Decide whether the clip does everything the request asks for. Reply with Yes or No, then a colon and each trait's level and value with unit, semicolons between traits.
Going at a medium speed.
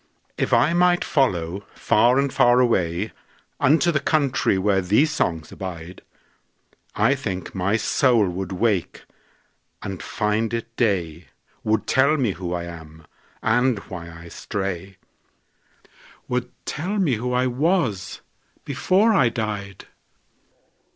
No: slow, 115 wpm